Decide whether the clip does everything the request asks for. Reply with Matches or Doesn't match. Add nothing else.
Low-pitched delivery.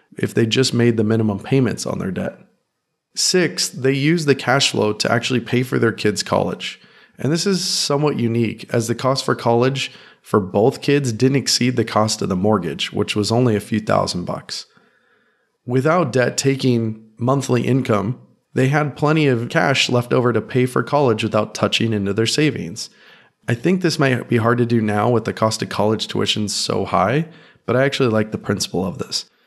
Matches